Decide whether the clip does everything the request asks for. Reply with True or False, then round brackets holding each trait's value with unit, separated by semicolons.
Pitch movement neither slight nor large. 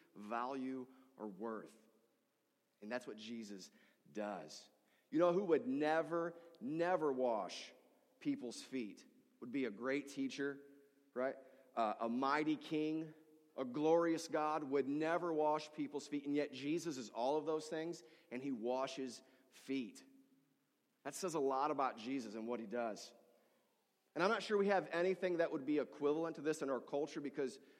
True (4.0 semitones)